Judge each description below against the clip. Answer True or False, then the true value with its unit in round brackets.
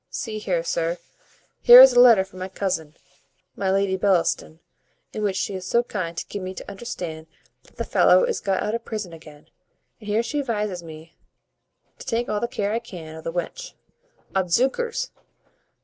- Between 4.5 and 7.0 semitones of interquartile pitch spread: True (5.2 semitones)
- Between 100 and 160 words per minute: False (185 wpm)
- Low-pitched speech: False (195 Hz)